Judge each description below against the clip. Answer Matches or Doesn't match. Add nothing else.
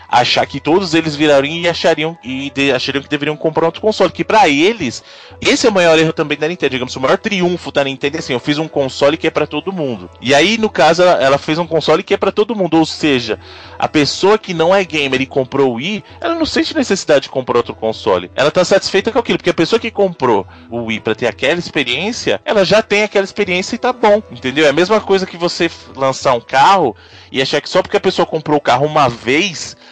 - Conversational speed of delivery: Doesn't match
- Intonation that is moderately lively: Doesn't match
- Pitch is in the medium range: Matches